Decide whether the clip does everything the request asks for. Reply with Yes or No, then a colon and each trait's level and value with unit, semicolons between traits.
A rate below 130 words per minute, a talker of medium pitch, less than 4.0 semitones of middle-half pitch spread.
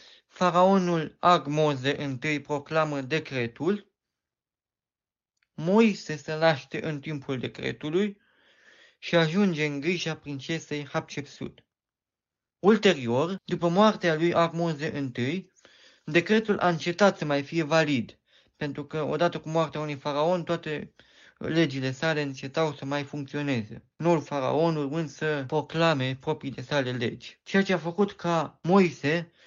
Yes: average, 120 wpm; medium, 160 Hz; average, 3.3 semitones